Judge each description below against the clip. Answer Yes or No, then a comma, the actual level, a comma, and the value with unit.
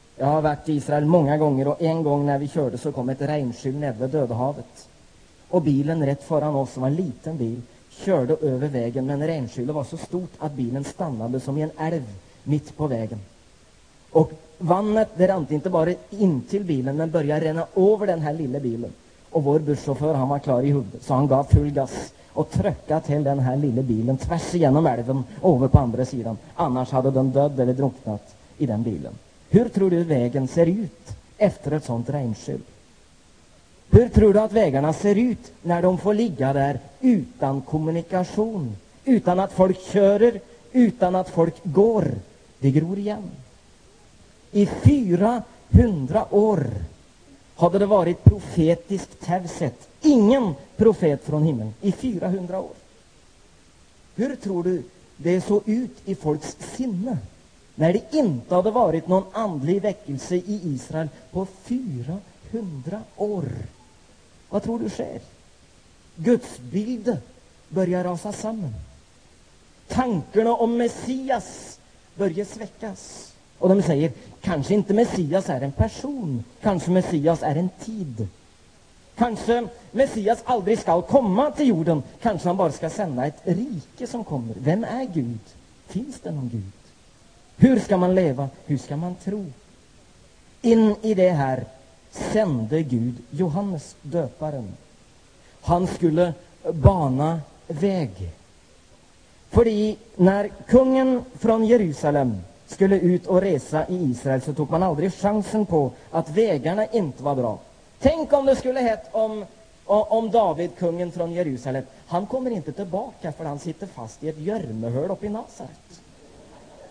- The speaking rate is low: No, average, 150 wpm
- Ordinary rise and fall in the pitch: No, wide, 6.8 semitones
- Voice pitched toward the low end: No, medium, 165 Hz